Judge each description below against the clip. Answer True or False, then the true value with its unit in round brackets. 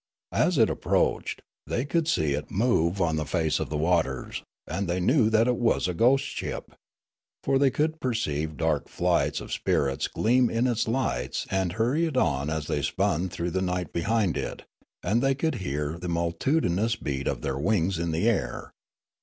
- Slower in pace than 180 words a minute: False (185 wpm)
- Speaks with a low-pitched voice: True (90 Hz)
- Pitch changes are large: True (7.2 semitones)